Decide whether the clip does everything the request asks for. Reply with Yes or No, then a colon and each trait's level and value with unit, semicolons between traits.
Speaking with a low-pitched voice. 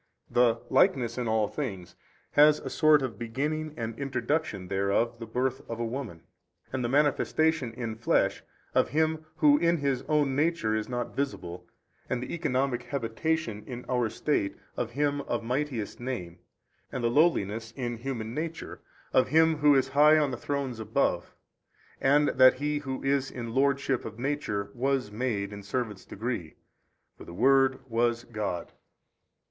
Yes: low, 125 Hz